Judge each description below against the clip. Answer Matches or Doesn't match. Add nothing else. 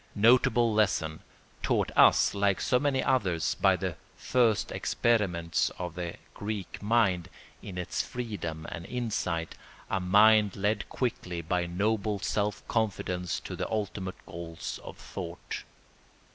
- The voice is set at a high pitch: Doesn't match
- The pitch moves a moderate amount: Matches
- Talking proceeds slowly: Matches